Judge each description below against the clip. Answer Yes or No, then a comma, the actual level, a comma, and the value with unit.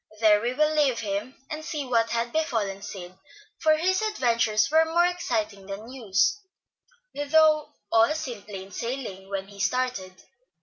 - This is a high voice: Yes, high, 235 Hz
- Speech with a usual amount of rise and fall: No, wide, 7.2 semitones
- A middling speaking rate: Yes, average, 155 wpm